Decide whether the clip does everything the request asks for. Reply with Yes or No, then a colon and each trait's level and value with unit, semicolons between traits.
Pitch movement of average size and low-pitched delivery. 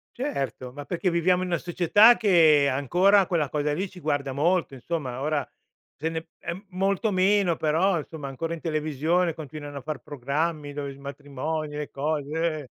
No: average, 3.7 semitones; medium, 155 Hz